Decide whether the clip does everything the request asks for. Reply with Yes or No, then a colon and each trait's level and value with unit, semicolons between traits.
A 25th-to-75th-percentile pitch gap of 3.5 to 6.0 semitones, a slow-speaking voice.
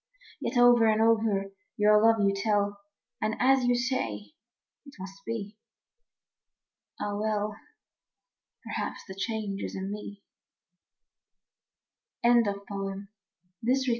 No: narrow, 2.5 semitones; slow, 120 wpm